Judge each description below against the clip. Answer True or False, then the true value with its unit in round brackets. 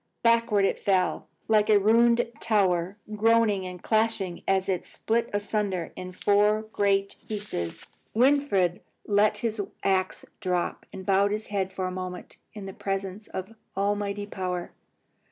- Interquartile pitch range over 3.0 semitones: False (2.4 semitones)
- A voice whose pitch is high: True (200 Hz)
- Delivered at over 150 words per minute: False (140 wpm)